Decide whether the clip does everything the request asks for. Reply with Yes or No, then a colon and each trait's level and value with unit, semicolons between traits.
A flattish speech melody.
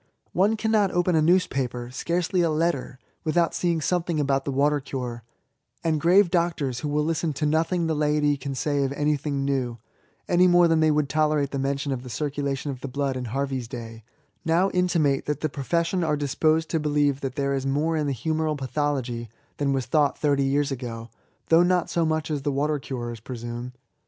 No: average, 3.1 semitones